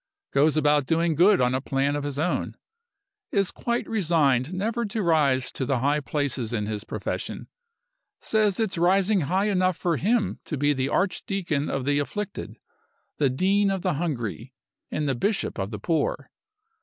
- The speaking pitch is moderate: Yes, medium, 155 Hz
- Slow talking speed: No, average, 170 wpm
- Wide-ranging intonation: Yes, wide, 5.9 semitones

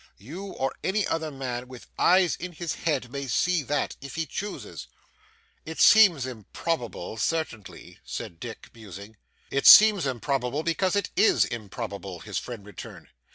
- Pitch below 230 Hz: Yes, low, 135 Hz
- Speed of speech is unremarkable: Yes, average, 150 wpm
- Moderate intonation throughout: No, wide, 6.5 semitones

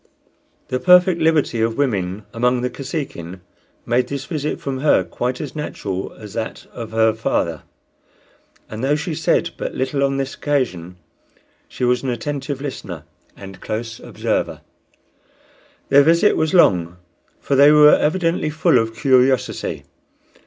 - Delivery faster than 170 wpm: No, average, 145 wpm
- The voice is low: Yes, low, 130 Hz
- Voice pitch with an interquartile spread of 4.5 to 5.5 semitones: Yes, average, 4.9 semitones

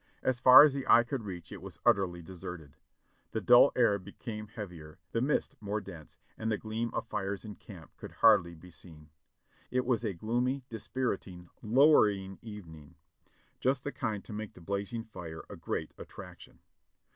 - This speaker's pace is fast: No, average, 170 wpm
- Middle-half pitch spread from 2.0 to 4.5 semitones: No, average, 4.9 semitones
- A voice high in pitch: No, low, 105 Hz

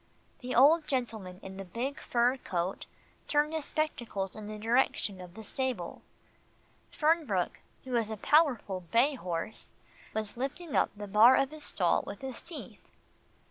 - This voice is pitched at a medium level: No, high, 235 Hz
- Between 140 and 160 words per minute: Yes, average, 155 wpm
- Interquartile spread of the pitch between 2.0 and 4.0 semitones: No, wide, 5.5 semitones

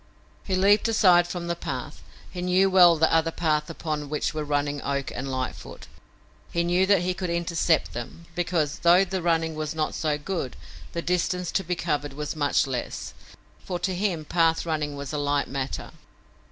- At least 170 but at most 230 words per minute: Yes, average, 185 wpm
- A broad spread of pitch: No, average, 3.2 semitones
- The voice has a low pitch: No, medium, 165 Hz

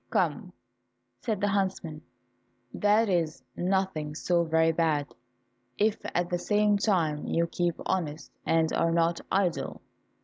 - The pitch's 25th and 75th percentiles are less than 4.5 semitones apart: Yes, average, 3.2 semitones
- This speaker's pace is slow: Yes, slow, 130 wpm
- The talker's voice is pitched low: No, medium, 175 Hz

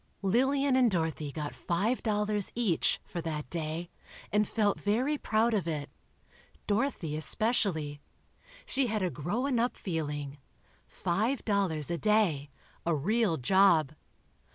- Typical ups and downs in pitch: No, wide, 6.0 semitones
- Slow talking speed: Yes, slow, 125 wpm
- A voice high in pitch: Yes, high, 195 Hz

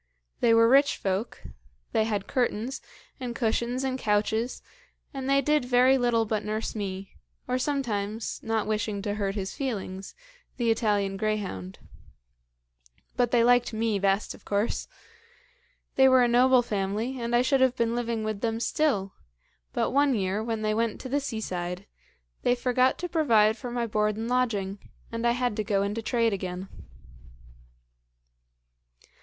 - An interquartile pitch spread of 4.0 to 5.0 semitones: No, average, 3.2 semitones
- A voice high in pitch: Yes, high, 225 Hz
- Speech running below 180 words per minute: Yes, average, 160 wpm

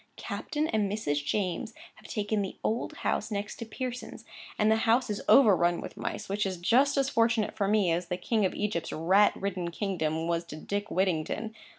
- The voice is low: No, high, 205 Hz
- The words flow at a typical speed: Yes, average, 190 wpm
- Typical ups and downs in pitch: Yes, average, 3.9 semitones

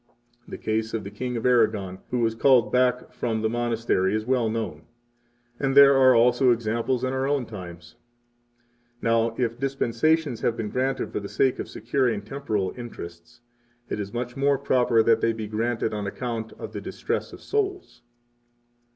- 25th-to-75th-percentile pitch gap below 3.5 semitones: Yes, average, 2.8 semitones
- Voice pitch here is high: No, low, 115 Hz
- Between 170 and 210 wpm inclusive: Yes, average, 175 wpm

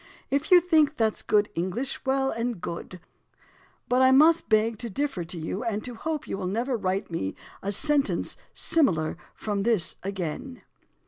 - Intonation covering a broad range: Yes, wide, 6.1 semitones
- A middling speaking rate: Yes, average, 170 wpm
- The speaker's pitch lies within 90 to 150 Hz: No, high, 230 Hz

